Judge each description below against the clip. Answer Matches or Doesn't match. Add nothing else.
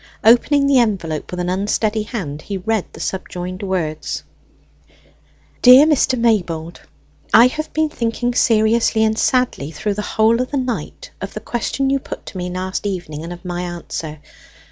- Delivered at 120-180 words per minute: Matches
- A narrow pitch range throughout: Doesn't match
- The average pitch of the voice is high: Matches